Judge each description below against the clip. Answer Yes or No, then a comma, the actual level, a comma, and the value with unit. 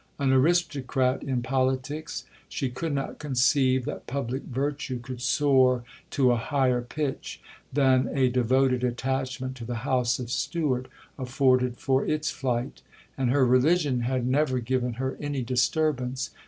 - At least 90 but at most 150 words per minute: Yes, average, 140 wpm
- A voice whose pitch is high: No, low, 130 Hz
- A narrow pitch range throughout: Yes, narrow, 1.9 semitones